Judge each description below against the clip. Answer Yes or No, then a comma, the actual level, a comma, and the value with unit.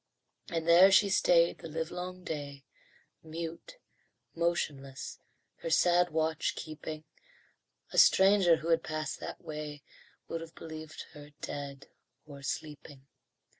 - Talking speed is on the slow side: Yes, slow, 120 wpm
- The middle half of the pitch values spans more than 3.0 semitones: No, narrow, 2.4 semitones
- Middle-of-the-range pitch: Yes, medium, 160 Hz